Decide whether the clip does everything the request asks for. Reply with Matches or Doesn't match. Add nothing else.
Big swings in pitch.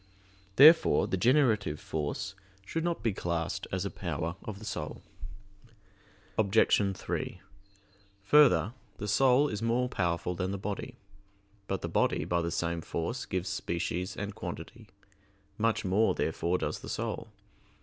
Doesn't match